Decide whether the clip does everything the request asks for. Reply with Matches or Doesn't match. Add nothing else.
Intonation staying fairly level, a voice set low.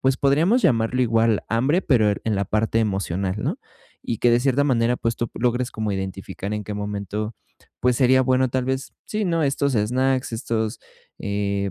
Doesn't match